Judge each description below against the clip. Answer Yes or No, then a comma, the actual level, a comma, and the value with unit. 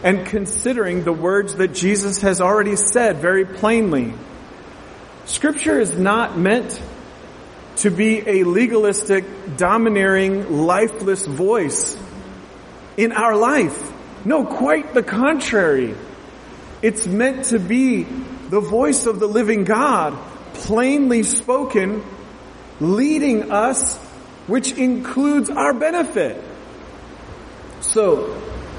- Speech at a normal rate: No, slow, 100 wpm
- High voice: Yes, high, 215 Hz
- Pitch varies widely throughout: No, average, 4.3 semitones